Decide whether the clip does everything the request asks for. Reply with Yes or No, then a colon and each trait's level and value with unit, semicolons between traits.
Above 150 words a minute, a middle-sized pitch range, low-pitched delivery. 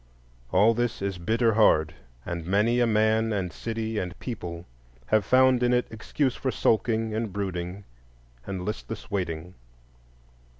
No: average, 140 wpm; average, 3.7 semitones; low, 110 Hz